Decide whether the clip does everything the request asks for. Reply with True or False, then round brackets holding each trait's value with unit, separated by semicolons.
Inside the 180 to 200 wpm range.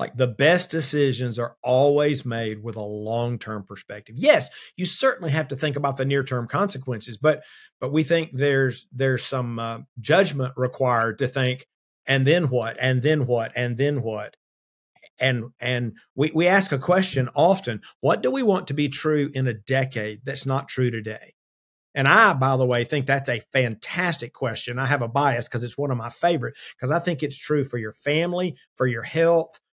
True (195 wpm)